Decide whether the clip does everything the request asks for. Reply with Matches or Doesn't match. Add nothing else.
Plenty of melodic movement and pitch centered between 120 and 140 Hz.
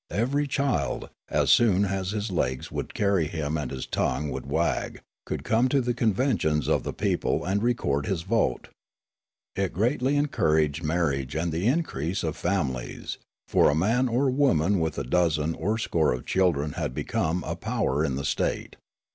Doesn't match